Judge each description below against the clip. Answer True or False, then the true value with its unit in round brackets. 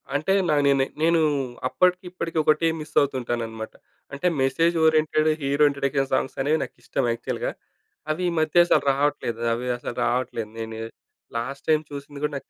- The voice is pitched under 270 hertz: True (140 Hz)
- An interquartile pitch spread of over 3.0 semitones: True (3.4 semitones)